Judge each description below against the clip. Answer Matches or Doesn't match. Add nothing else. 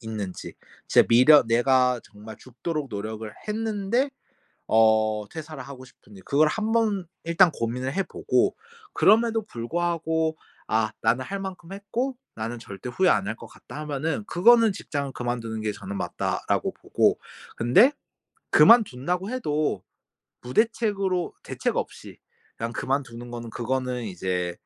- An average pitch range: Doesn't match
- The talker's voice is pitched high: Doesn't match